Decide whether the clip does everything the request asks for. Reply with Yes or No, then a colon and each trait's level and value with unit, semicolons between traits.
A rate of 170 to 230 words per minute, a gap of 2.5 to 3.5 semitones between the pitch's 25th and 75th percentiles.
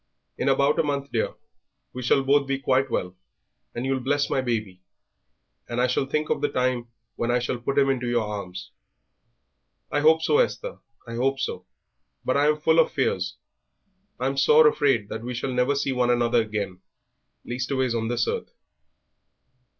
Yes: average, 180 wpm; average, 2.8 semitones